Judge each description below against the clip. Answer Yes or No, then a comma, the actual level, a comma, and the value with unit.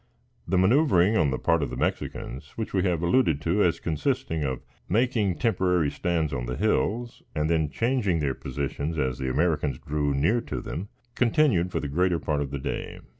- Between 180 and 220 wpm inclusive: Yes, average, 190 wpm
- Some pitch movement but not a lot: No, wide, 6.0 semitones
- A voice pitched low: Yes, very low, 85 Hz